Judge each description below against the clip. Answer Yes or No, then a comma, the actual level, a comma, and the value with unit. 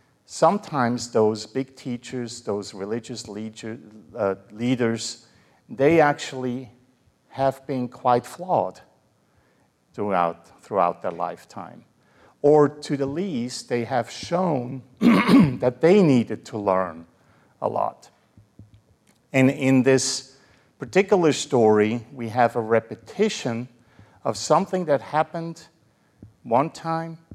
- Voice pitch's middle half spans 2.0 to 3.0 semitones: No, average, 4.4 semitones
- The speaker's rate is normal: No, slow, 100 wpm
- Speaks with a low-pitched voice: Yes, low, 125 Hz